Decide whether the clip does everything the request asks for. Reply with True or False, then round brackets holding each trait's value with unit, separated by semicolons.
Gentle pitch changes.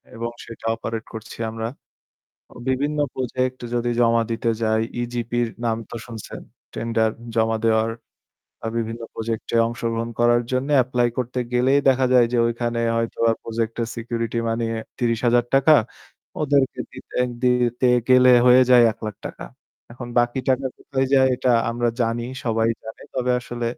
True (1.8 semitones)